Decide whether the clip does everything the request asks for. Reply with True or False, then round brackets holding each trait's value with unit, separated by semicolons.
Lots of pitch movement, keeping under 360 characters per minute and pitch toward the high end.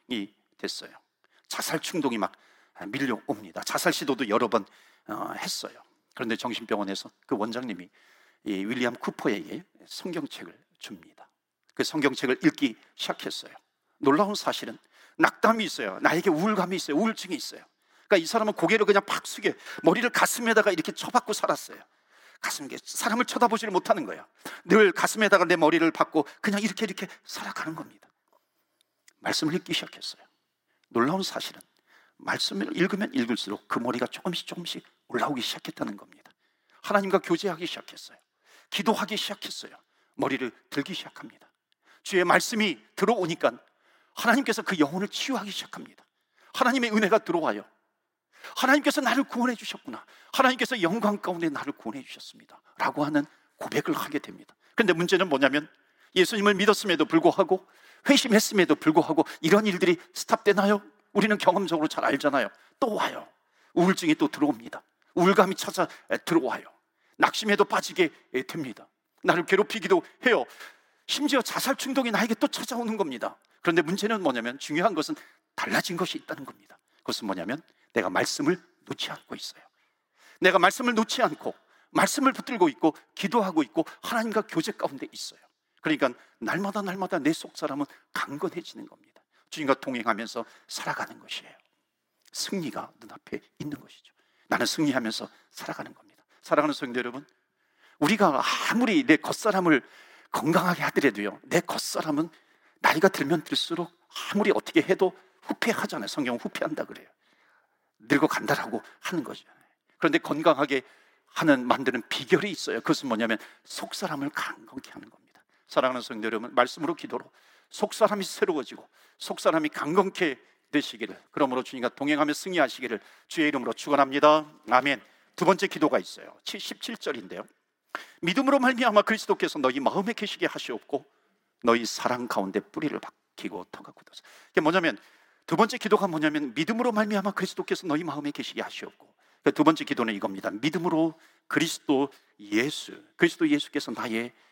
False (6.4 semitones; 375 characters per minute; 200 Hz)